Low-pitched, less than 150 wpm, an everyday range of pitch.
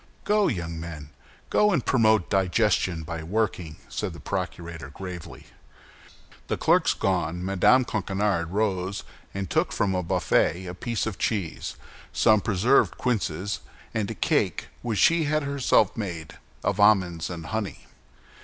Yes: very low, 95 Hz; average, 140 wpm; average, 4.2 semitones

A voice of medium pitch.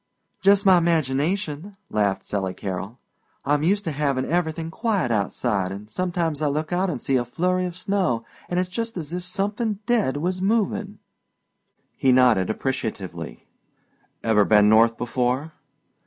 Yes: medium, 155 Hz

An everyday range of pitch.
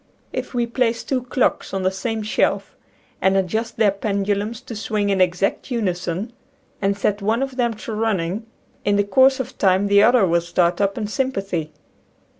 Yes: average, 3.2 semitones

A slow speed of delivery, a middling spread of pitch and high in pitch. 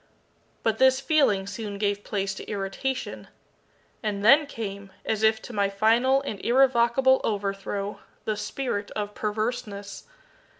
Yes: slow, 130 wpm; average, 3.6 semitones; high, 215 Hz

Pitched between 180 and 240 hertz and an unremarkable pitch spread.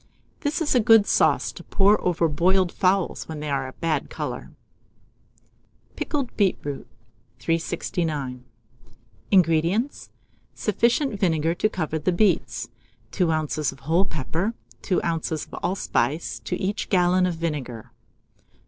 No: medium, 170 Hz; average, 3.9 semitones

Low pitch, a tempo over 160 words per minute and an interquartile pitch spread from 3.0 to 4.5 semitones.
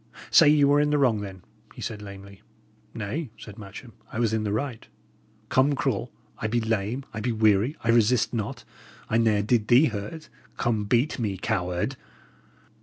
Yes: low, 110 Hz; average, 180 wpm; average, 3.6 semitones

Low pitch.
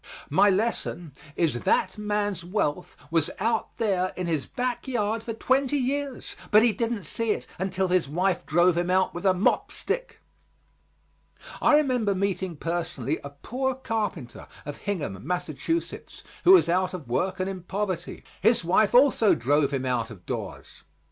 No: high, 190 Hz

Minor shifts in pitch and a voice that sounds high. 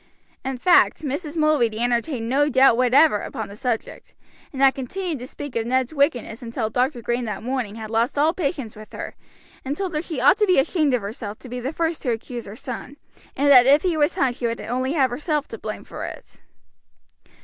No: average, 3.9 semitones; very high, 260 Hz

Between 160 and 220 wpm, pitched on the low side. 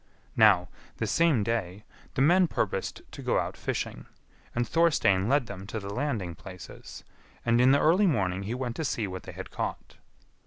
Yes: average, 185 wpm; low, 115 Hz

